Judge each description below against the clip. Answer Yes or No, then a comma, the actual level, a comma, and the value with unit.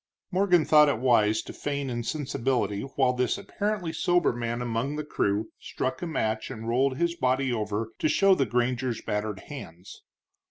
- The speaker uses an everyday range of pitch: Yes, average, 4.9 semitones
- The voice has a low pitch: Yes, low, 130 Hz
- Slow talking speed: No, average, 165 wpm